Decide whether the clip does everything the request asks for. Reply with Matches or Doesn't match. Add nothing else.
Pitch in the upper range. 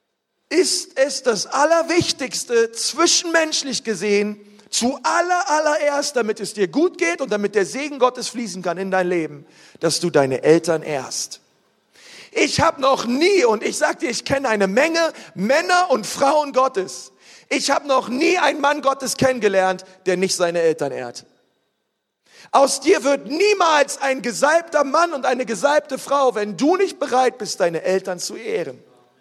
Matches